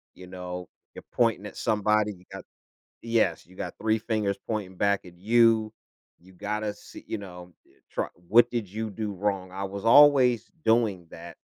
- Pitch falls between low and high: No, low, 105 Hz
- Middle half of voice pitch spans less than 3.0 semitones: No, average, 3.3 semitones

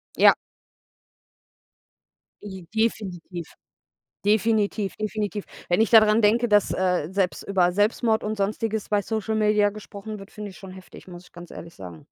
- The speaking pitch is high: Yes, high, 205 Hz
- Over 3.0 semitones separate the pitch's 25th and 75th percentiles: No, narrow, 2.5 semitones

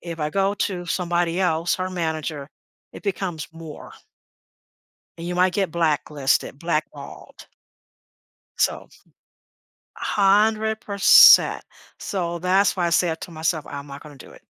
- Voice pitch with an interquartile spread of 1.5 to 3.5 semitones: Yes, average, 3.1 semitones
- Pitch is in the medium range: Yes, medium, 170 Hz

